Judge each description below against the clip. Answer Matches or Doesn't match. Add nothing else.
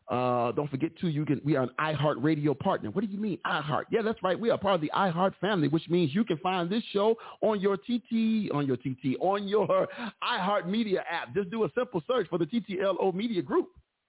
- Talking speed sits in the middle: Doesn't match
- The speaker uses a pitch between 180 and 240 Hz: Matches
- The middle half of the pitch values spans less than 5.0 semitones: Doesn't match